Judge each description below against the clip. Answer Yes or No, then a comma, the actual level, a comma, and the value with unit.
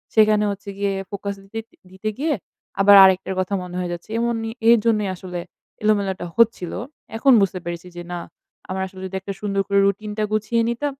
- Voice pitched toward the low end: No, high, 200 Hz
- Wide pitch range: No, narrow, 2.5 semitones